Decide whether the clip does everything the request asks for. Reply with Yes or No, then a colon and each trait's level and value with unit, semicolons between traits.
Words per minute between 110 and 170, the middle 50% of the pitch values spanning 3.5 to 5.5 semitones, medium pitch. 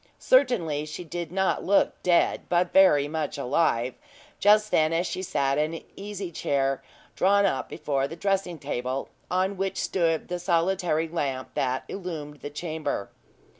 Yes: average, 155 wpm; average, 4.5 semitones; medium, 165 Hz